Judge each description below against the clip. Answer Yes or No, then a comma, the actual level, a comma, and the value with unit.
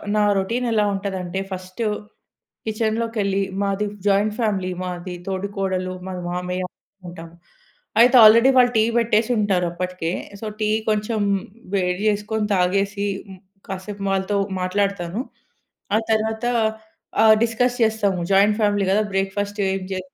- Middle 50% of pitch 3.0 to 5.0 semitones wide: No, narrow, 2.5 semitones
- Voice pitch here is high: Yes, high, 200 Hz